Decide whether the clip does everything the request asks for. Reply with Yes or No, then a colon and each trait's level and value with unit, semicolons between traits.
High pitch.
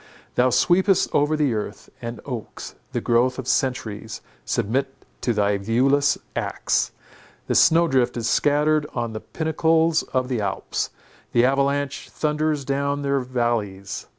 No: low, 130 Hz